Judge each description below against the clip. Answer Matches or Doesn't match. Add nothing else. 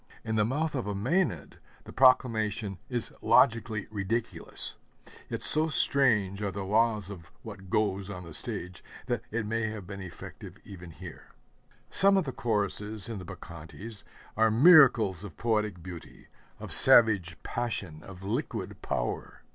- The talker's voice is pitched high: Doesn't match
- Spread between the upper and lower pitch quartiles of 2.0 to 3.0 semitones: Doesn't match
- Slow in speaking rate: Doesn't match